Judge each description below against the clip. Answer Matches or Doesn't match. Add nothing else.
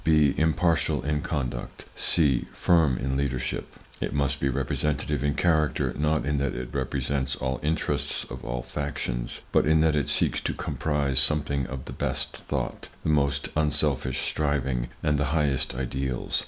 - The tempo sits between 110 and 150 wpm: Doesn't match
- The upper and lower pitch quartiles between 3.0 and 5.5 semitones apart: Doesn't match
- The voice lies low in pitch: Matches